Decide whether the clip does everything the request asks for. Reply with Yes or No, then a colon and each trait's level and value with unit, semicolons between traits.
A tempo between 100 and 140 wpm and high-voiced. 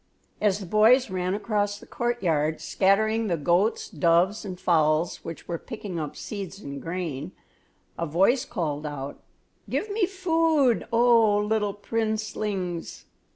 Yes: slow, 135 wpm; high, 200 Hz